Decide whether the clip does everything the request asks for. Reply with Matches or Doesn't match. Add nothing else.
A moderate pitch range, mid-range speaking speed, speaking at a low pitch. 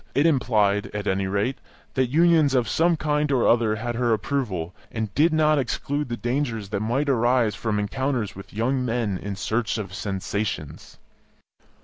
Matches